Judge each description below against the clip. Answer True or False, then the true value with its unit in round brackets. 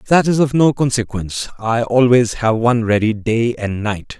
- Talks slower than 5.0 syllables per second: True (4.7 syllables/s)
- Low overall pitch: True (115 Hz)